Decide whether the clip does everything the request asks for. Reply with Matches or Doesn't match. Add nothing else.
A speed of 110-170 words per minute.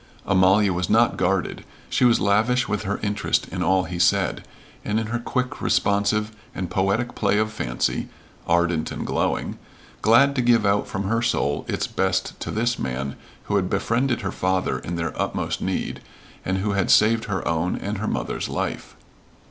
Doesn't match